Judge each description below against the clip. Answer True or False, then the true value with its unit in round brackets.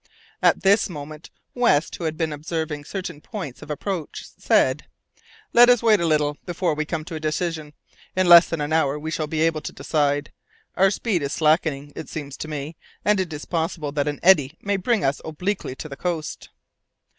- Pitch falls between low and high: True (160 Hz)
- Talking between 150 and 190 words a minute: False (205 wpm)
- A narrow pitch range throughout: False (3.2 semitones)